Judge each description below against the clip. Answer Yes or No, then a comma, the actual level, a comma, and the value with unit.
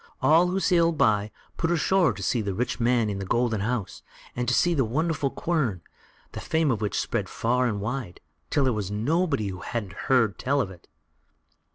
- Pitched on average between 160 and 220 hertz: No, low, 125 Hz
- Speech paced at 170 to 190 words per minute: No, average, 200 wpm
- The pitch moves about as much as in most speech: No, wide, 6.9 semitones